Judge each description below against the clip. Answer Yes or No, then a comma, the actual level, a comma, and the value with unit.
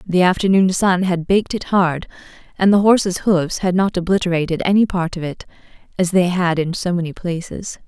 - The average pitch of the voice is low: No, medium, 180 Hz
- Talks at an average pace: Yes, average, 190 wpm